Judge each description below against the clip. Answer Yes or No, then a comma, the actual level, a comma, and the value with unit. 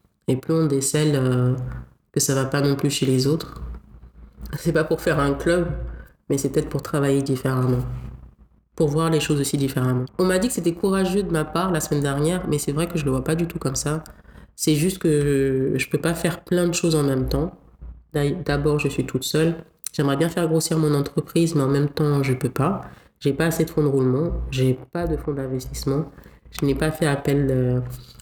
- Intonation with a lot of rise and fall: No, average, 3.7 semitones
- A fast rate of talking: Yes, fast, 230 wpm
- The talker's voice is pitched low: No, medium, 145 Hz